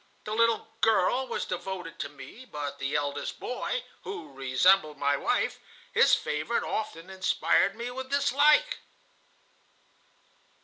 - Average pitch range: No, wide, 9.0 semitones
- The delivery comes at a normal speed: No, slow, 125 wpm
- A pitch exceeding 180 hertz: Yes, high, 190 Hz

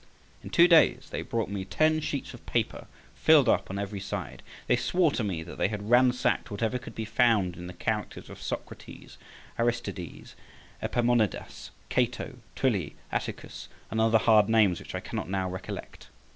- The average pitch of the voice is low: Yes, low, 115 Hz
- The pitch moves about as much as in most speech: Yes, average, 3.9 semitones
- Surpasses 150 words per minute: Yes, average, 170 wpm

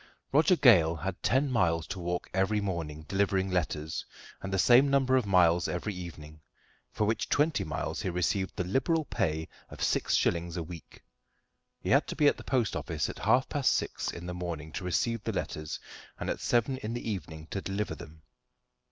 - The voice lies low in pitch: Yes, very low, 95 Hz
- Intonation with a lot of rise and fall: Yes, wide, 5.7 semitones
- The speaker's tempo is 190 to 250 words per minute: Yes, average, 195 wpm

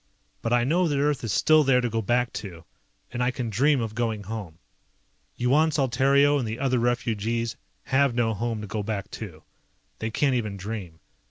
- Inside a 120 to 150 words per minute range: No, average, 190 wpm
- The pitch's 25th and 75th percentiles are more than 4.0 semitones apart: No, average, 3.5 semitones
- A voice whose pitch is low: Yes, low, 120 Hz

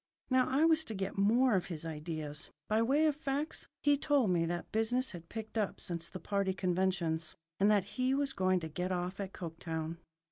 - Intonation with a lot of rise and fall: Yes, wide, 6.8 semitones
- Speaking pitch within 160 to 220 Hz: Yes, high, 190 Hz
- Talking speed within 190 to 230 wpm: Yes, fast, 205 wpm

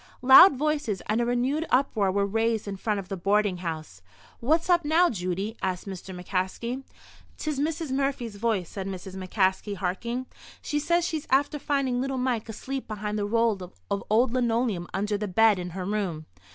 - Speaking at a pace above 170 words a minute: Yes, average, 180 wpm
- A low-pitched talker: No, high, 215 Hz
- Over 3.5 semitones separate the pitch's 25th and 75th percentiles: Yes, wide, 5.4 semitones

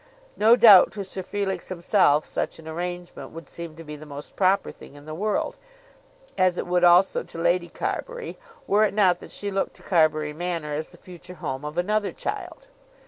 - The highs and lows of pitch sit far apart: No, average, 3.7 semitones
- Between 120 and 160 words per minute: No, average, 195 wpm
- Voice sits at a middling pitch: Yes, medium, 175 Hz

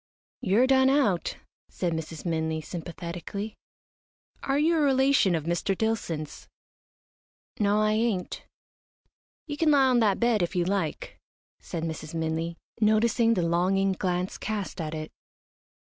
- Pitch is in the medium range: No, high, 195 Hz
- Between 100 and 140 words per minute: Yes, slow, 135 wpm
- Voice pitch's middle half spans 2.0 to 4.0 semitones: No, wide, 5.4 semitones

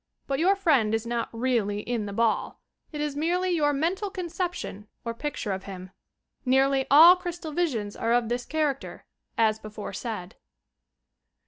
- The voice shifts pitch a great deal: Yes, wide, 6.5 semitones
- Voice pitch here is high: Yes, very high, 260 Hz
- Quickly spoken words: No, average, 155 wpm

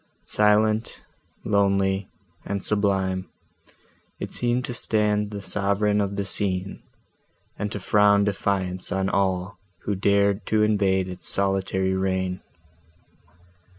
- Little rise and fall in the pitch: Yes, narrow, 1.5 semitones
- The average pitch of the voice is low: Yes, low, 100 Hz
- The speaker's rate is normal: No, slow, 115 wpm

